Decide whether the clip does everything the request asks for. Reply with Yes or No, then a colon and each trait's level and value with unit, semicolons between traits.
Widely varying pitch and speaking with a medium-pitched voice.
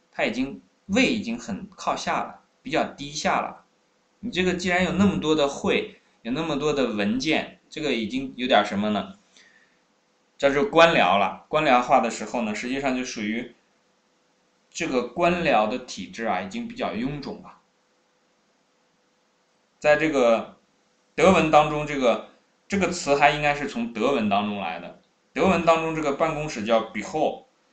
Yes: wide, 6.2 semitones; medium, 160 Hz